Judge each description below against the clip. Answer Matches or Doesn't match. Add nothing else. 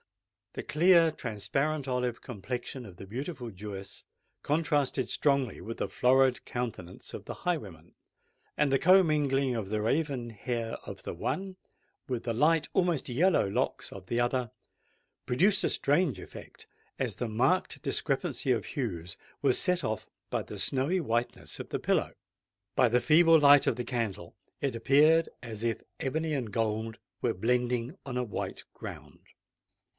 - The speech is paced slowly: Doesn't match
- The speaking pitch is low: Matches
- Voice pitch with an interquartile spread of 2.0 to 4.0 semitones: Doesn't match